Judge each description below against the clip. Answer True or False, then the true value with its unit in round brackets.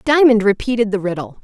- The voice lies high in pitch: True (215 Hz)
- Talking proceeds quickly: False (170 wpm)